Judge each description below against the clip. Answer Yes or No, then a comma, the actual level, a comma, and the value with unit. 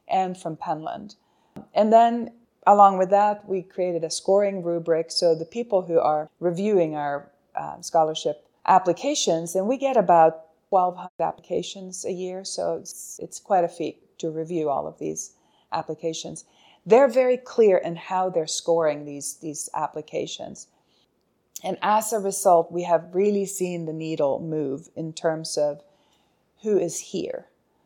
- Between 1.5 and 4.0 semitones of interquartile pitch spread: Yes, average, 3.5 semitones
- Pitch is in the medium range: Yes, medium, 170 Hz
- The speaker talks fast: No, average, 150 wpm